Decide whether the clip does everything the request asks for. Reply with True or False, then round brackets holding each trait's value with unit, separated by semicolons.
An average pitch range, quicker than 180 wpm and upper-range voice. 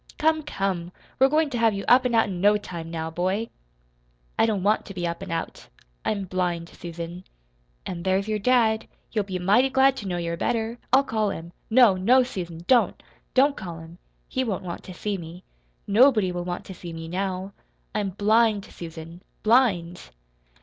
True (4.6 semitones; 190 wpm; 195 Hz)